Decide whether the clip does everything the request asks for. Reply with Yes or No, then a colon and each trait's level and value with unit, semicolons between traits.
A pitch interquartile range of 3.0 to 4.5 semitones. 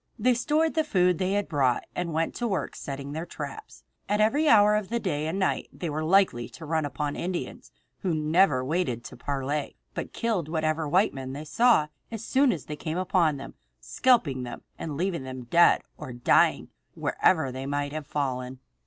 No: wide, 5.6 semitones